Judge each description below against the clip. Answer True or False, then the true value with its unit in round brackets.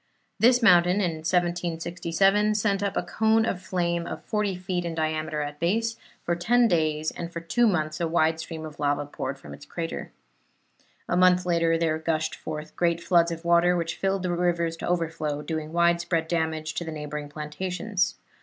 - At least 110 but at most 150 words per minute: False (180 wpm)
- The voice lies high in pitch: False (170 Hz)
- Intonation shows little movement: True (2.3 semitones)